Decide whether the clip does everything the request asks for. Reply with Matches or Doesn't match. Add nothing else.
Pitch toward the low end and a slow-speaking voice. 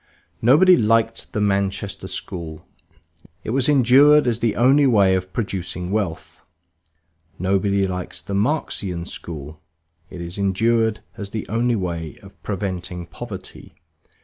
Matches